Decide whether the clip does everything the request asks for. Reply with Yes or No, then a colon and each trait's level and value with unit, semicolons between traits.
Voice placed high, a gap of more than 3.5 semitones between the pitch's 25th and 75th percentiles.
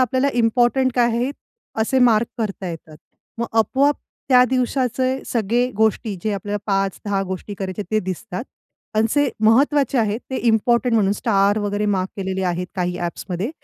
Yes: high, 220 Hz; average, 4.2 semitones